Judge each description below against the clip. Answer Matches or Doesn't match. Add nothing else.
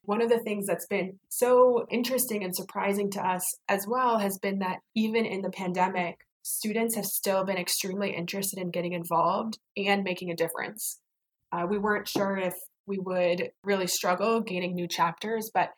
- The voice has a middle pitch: Doesn't match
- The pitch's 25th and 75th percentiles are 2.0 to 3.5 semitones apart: Matches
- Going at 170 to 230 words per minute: Matches